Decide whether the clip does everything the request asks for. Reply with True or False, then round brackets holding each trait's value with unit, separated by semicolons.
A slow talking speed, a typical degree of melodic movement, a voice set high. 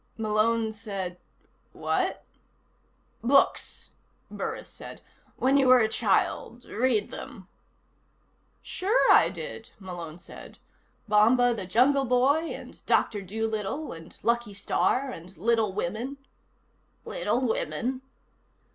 True (110 wpm; 4.1 semitones; 225 Hz)